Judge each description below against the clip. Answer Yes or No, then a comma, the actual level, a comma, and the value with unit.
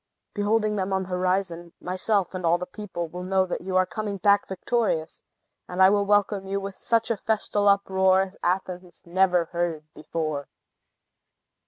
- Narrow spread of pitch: Yes, narrow, 2.3 semitones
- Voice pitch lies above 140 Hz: Yes, high, 190 Hz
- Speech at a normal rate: Yes, average, 165 wpm